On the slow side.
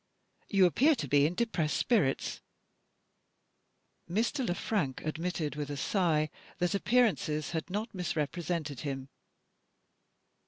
Yes: slow, 115 wpm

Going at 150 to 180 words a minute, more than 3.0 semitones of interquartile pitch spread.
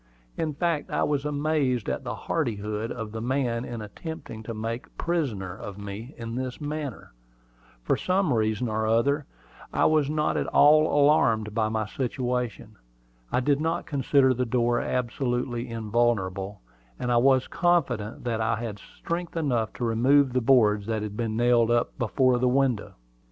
Yes: average, 165 wpm; average, 4.2 semitones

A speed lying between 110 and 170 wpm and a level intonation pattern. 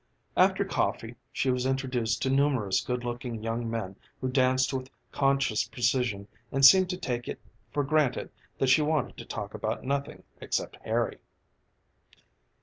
Yes: average, 150 wpm; narrow, 2.3 semitones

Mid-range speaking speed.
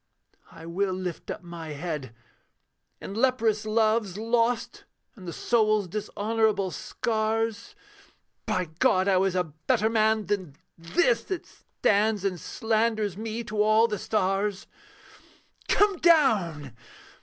No: slow, 120 wpm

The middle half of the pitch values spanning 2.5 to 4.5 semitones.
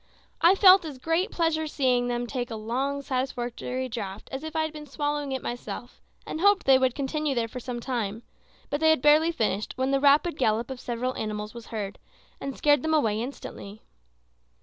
Yes: average, 4.0 semitones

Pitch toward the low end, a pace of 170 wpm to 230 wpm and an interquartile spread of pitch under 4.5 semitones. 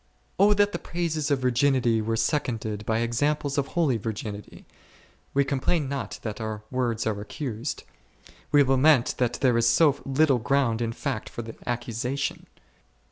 No: low, 130 Hz; average, 155 wpm; average, 3.9 semitones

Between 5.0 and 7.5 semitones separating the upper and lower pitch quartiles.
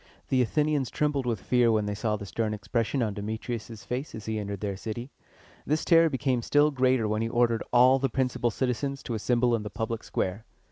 No: average, 3.2 semitones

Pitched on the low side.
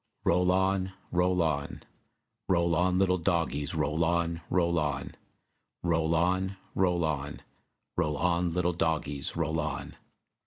Yes: very low, 85 Hz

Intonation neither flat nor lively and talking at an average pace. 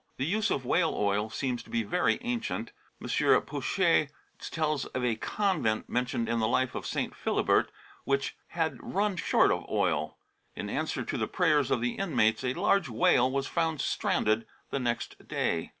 No: wide, 6.3 semitones; average, 175 wpm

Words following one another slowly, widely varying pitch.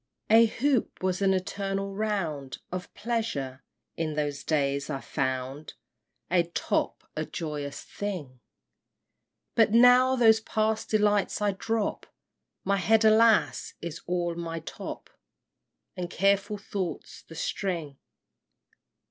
Yes: slow, 120 wpm; wide, 5.7 semitones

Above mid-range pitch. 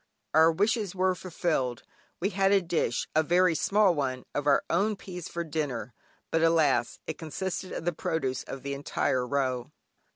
No: medium, 160 Hz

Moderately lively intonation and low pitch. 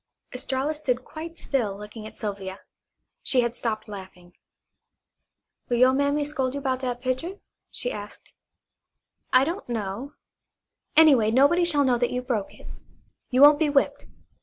No: average, 4.1 semitones; very high, 255 Hz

